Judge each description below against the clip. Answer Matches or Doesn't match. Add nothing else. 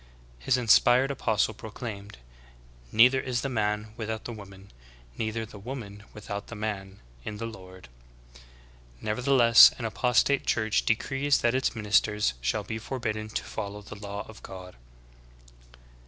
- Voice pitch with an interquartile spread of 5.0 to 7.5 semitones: Doesn't match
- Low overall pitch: Matches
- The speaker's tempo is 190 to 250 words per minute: Doesn't match